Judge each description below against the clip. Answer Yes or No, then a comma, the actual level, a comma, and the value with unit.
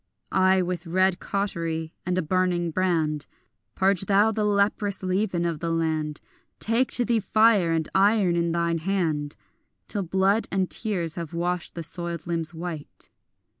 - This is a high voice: No, medium, 180 Hz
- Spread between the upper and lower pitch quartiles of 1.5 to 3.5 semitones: Yes, average, 2.9 semitones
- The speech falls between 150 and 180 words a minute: Yes, average, 155 wpm